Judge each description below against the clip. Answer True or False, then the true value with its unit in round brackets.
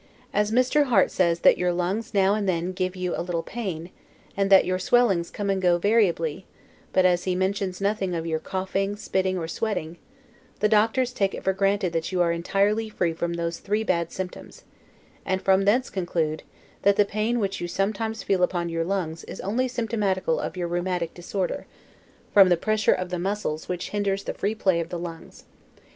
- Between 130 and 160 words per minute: False (195 wpm)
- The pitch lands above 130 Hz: True (190 Hz)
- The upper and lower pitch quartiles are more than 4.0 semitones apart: False (2.9 semitones)